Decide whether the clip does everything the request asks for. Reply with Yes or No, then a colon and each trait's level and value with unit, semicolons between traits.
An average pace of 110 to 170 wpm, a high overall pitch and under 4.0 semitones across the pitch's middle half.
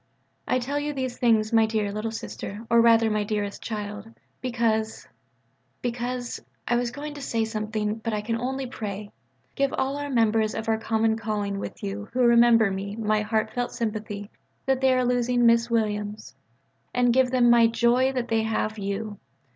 No: average, 180 wpm; high, 225 Hz; narrow, 2.4 semitones